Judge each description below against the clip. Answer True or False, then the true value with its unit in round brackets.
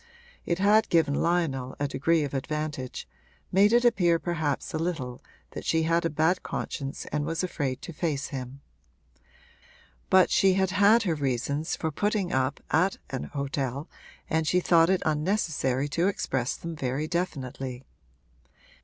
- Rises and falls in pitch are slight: False (4.3 semitones)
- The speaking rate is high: False (155 wpm)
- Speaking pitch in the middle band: True (160 Hz)